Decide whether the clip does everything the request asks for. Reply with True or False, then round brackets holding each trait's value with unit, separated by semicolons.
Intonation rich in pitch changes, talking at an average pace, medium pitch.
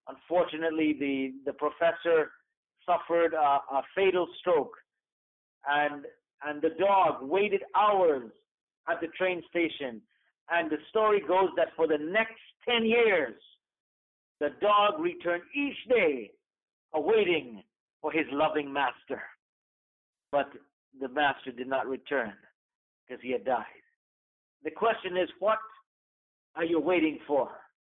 False (7.0 semitones; 120 wpm; 165 Hz)